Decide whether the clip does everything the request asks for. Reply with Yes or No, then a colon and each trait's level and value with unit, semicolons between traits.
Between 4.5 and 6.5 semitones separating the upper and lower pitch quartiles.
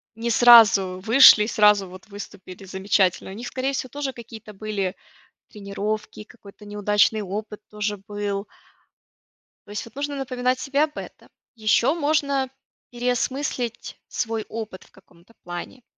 No: average, 3.6 semitones